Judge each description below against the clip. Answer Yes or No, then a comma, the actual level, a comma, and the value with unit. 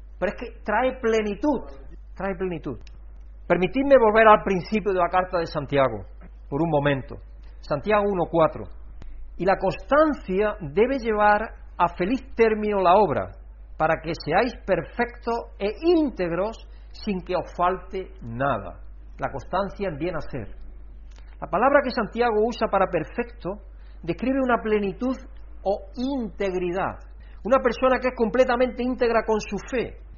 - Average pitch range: No, wide, 6.5 semitones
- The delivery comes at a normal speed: Yes, average, 135 wpm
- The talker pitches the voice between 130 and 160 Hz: No, high, 195 Hz